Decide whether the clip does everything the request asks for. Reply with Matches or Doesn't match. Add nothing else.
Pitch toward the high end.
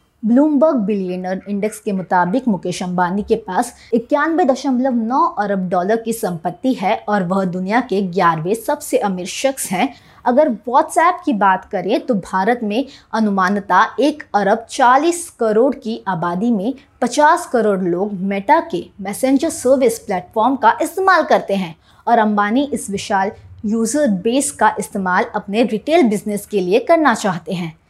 Matches